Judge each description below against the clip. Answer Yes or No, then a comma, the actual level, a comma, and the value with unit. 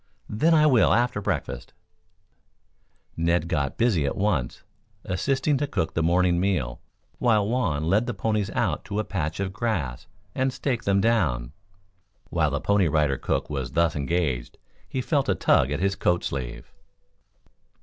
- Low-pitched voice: Yes, very low, 95 Hz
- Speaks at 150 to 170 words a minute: Yes, average, 160 wpm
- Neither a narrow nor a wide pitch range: No, wide, 6.7 semitones